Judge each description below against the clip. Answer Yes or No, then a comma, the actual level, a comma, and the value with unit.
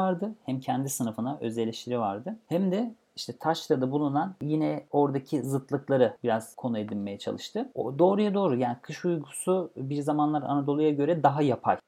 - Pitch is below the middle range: No, medium, 145 Hz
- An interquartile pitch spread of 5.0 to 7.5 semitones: Yes, wide, 5.4 semitones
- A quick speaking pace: Yes, fast, 155 wpm